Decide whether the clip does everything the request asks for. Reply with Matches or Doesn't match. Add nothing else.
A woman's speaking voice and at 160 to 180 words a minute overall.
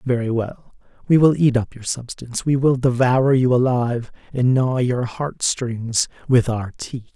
Doesn't match